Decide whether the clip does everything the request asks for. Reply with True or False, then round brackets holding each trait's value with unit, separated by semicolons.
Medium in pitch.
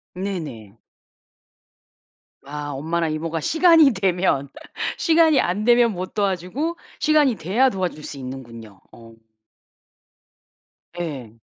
True (175 Hz)